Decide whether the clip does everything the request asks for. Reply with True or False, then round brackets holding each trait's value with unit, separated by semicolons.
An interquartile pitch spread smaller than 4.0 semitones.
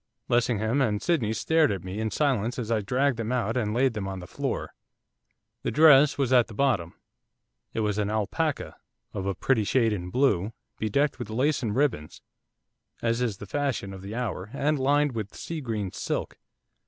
False (4.7 semitones)